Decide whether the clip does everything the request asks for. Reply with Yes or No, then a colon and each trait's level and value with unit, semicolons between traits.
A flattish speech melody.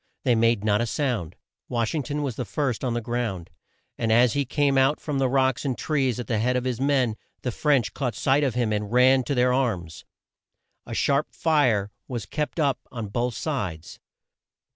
No: average, 3.4 semitones